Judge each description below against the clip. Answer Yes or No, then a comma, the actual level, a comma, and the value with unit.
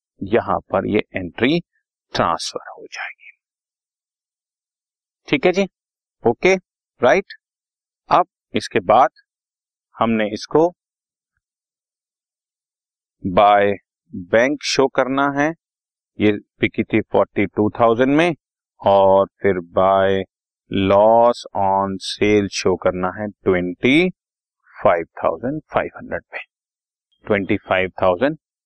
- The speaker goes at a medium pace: No, slow, 100 wpm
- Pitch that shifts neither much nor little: No, wide, 6.2 semitones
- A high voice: No, low, 105 Hz